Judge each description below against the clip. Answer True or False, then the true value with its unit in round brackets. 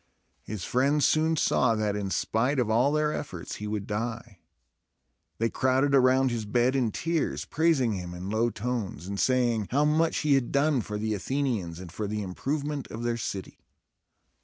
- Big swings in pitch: False (4.8 semitones)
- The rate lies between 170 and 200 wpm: True (180 wpm)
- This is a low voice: True (120 Hz)